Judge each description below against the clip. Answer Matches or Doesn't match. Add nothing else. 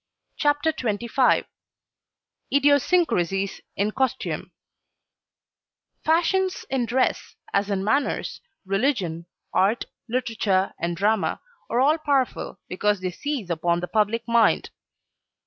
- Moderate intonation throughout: Doesn't match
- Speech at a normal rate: Doesn't match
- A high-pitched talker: Matches